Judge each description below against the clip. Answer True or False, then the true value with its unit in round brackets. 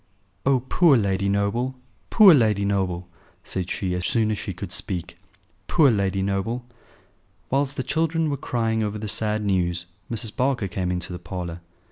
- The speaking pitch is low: True (105 Hz)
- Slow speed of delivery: False (165 wpm)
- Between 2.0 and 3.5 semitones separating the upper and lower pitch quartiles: False (5.0 semitones)